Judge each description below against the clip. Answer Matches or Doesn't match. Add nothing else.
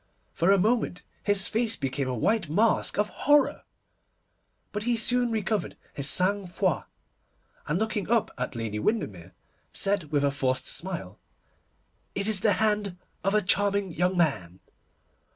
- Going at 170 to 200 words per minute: Doesn't match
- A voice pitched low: Doesn't match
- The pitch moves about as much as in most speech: Doesn't match